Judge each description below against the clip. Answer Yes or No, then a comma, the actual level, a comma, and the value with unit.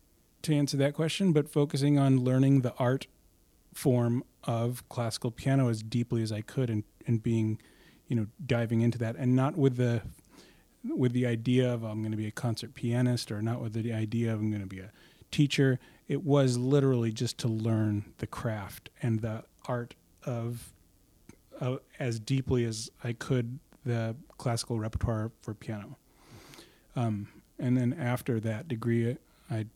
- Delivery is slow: No, average, 170 wpm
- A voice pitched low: Yes, low, 120 Hz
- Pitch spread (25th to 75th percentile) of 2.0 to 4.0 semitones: Yes, average, 2.8 semitones